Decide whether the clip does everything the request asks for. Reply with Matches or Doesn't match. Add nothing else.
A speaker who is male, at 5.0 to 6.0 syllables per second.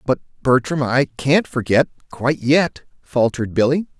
Doesn't match